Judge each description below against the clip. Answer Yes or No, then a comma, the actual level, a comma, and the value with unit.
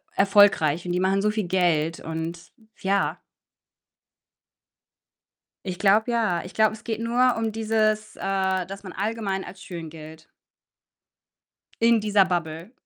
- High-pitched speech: Yes, high, 195 Hz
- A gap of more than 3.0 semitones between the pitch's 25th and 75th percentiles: Yes, average, 3.6 semitones